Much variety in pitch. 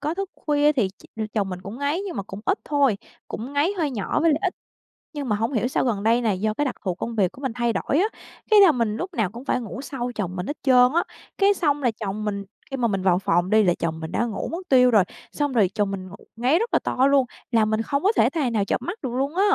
Yes: wide, 5.8 semitones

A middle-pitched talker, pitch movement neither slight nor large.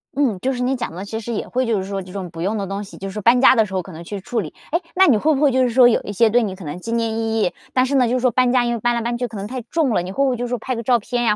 No: high, 230 Hz; average, 4.1 semitones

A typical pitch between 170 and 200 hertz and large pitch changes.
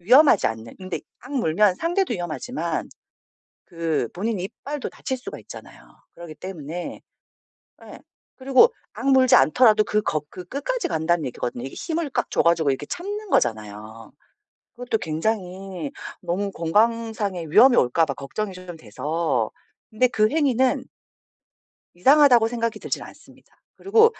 Yes: high, 195 Hz; wide, 7.9 semitones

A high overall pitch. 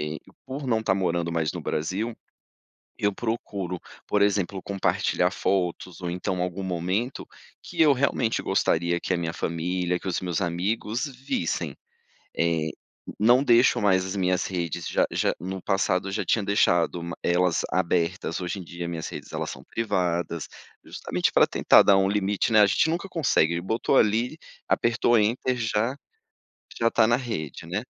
No: very low, 95 Hz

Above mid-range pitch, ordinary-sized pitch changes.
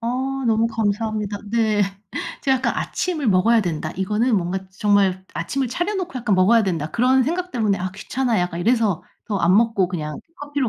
Yes: high, 220 Hz; average, 5.0 semitones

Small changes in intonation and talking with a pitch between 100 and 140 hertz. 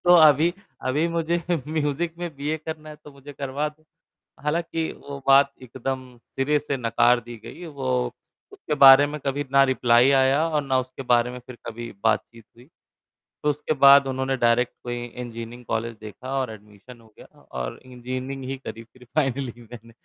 No: average, 3.6 semitones; low, 135 Hz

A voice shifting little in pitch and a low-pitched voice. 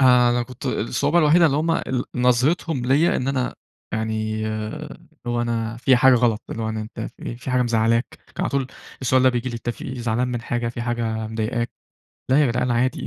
Yes: narrow, 2.1 semitones; low, 120 Hz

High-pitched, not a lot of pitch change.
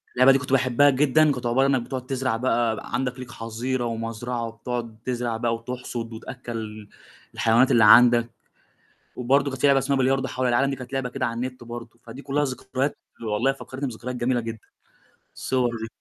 No: low, 125 Hz; narrow, 2.2 semitones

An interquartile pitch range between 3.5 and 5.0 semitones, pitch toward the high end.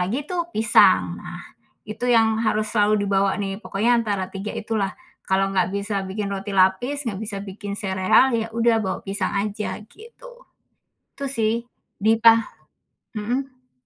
No: average, 3.0 semitones; high, 215 Hz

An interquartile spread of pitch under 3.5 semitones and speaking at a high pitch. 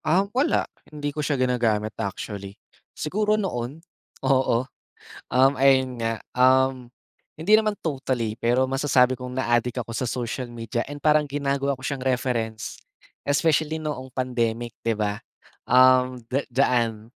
No: average, 3.1 semitones; low, 130 Hz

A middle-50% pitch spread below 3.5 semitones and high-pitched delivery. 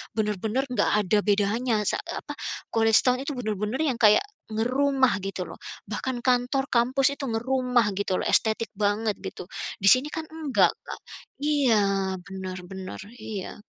No: average, 4.2 semitones; high, 225 Hz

